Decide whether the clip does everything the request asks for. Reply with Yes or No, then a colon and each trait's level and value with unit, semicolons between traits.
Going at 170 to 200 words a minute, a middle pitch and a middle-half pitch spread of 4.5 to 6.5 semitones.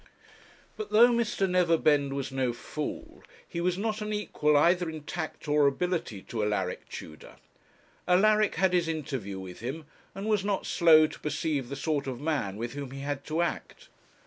Yes: average, 175 wpm; medium, 155 Hz; average, 5.1 semitones